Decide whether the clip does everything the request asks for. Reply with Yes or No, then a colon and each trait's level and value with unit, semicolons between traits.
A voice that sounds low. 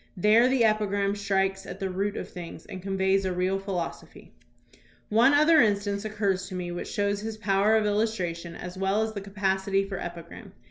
No: high, 195 Hz